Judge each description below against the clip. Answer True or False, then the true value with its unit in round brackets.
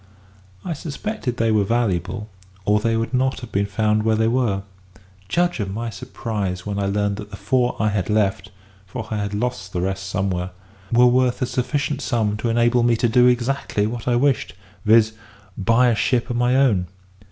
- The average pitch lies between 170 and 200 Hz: False (115 Hz)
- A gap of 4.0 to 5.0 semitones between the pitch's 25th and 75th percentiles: False (3.3 semitones)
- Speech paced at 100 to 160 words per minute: False (190 wpm)